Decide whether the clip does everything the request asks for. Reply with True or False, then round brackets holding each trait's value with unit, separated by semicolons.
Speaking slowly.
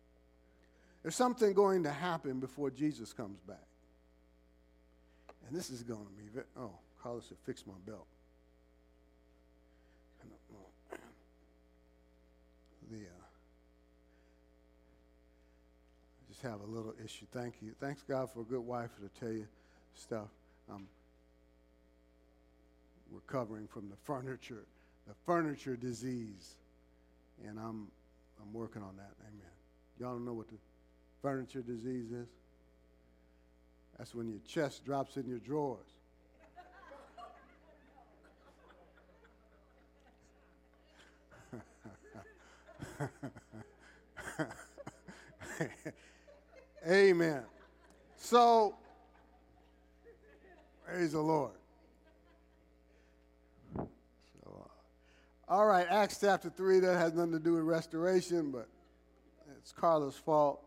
True (95 wpm)